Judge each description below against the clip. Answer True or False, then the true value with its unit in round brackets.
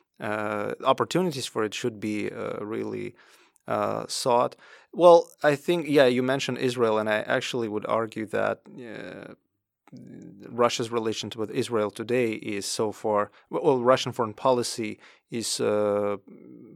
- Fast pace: False (140 wpm)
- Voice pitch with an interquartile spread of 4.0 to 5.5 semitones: False (3.3 semitones)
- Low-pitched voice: True (115 Hz)